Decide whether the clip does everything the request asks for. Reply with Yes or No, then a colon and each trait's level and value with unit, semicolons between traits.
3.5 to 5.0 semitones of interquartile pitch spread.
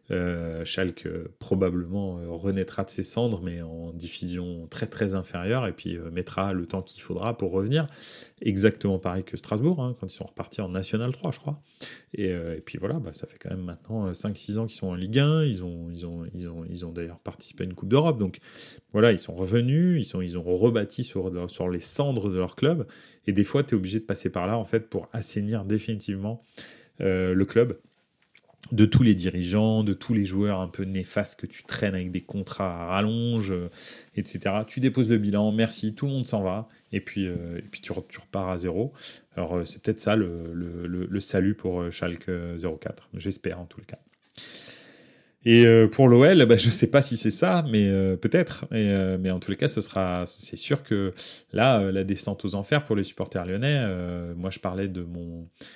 Yes: average, 3.9 semitones